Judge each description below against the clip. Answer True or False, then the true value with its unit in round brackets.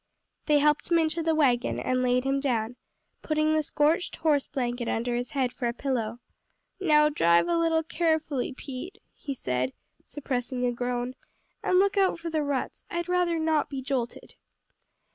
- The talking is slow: False (170 wpm)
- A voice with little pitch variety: False (4.4 semitones)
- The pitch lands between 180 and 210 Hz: False (280 Hz)